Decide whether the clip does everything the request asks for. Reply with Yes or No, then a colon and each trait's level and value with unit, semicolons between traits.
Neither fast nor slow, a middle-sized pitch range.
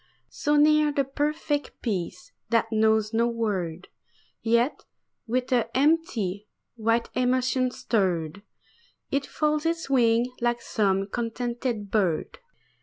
No: slow, 110 wpm; average, 4.2 semitones